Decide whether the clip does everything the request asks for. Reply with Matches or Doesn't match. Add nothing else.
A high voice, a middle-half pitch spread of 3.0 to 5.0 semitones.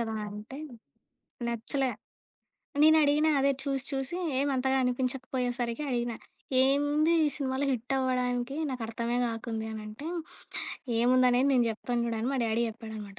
Doesn't match